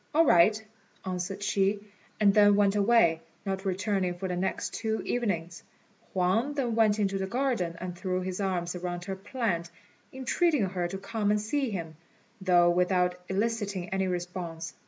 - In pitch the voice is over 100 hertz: Yes, high, 190 Hz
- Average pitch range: Yes, average, 3.0 semitones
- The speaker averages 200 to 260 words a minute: No, average, 160 wpm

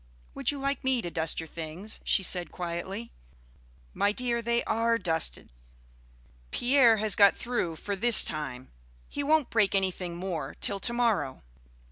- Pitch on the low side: No, high, 200 Hz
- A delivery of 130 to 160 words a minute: Yes, average, 155 wpm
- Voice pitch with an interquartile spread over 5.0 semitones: Yes, wide, 5.5 semitones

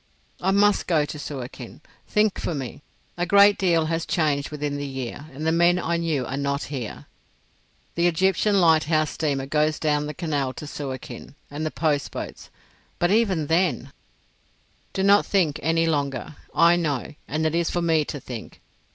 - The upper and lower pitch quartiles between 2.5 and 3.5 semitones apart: Yes, average, 3.2 semitones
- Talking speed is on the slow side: No, average, 170 wpm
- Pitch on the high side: No, medium, 155 Hz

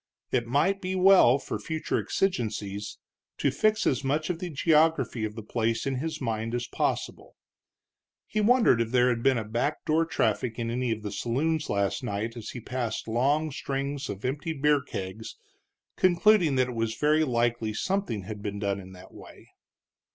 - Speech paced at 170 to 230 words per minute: Yes, average, 180 wpm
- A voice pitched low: Yes, low, 125 Hz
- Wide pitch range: Yes, wide, 5.7 semitones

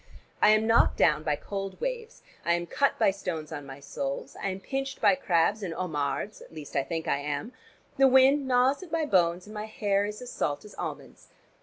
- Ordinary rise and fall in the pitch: No, wide, 7.9 semitones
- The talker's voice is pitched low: No, high, 195 Hz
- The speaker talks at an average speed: No, fast, 215 wpm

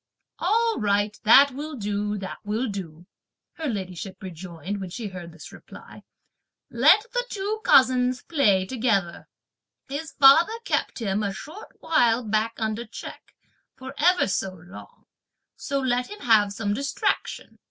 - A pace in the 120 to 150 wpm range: Yes, average, 140 wpm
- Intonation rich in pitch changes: Yes, wide, 5.9 semitones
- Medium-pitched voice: No, high, 225 Hz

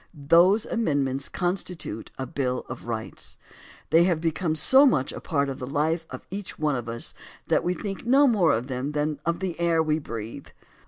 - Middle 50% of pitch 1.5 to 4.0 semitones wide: No, average, 4.9 semitones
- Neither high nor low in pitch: Yes, medium, 155 Hz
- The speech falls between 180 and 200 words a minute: Yes, average, 195 wpm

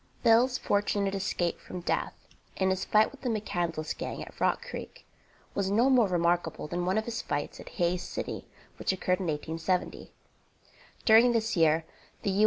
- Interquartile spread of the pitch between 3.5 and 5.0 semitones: Yes, average, 4.1 semitones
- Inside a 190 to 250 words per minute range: No, average, 180 wpm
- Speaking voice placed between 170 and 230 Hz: Yes, high, 190 Hz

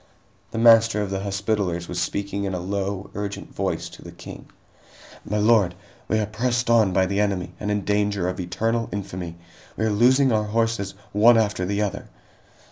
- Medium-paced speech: Yes, average, 185 wpm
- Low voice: Yes, low, 105 Hz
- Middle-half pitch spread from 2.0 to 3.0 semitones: Yes, narrow, 2.6 semitones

